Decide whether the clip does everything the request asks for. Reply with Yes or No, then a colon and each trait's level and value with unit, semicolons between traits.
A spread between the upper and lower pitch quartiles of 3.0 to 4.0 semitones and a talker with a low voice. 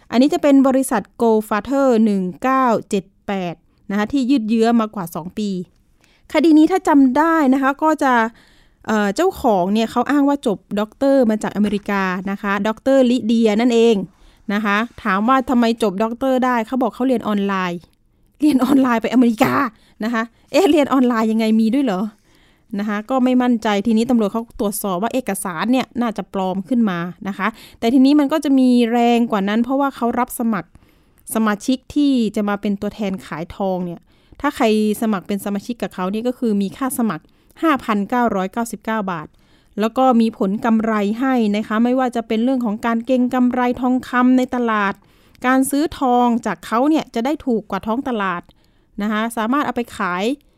No: average, 3.7 semitones; high, 230 Hz